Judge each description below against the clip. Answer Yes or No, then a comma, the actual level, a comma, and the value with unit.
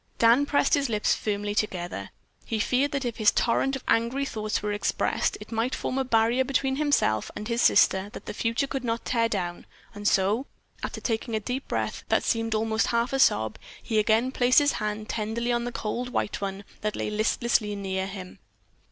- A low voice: No, high, 225 Hz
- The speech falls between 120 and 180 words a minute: No, average, 200 wpm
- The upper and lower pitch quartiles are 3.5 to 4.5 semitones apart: No, average, 3.1 semitones